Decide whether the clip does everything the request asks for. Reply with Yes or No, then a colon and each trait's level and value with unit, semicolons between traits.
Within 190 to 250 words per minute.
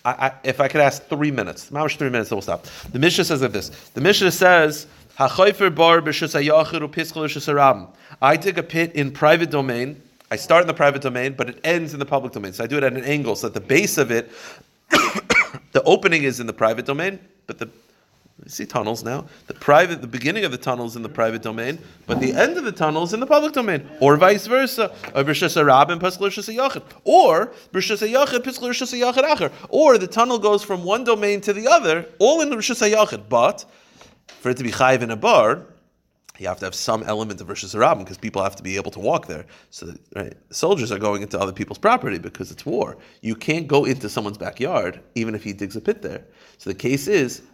Yes: fast, 205 wpm